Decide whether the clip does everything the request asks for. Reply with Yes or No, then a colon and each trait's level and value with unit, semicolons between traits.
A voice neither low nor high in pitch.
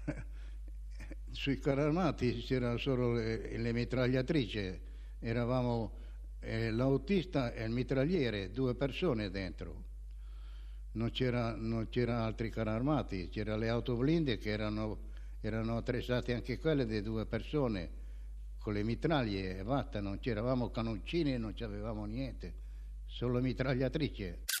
No: low, 115 Hz